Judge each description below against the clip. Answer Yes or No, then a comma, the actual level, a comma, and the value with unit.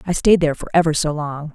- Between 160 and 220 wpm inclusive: No, fast, 270 wpm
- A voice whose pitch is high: No, medium, 155 Hz